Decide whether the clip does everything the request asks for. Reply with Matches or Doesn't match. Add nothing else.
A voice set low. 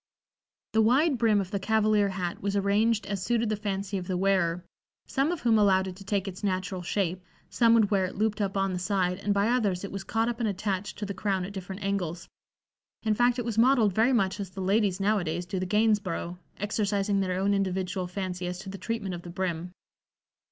Doesn't match